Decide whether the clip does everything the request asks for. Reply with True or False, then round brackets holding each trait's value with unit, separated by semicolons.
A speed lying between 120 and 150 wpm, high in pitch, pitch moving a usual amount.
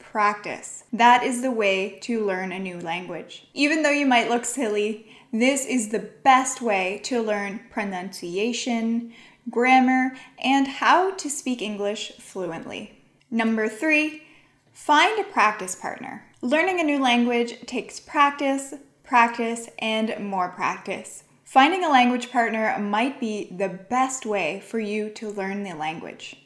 True (140 wpm; 235 Hz; 4.0 semitones)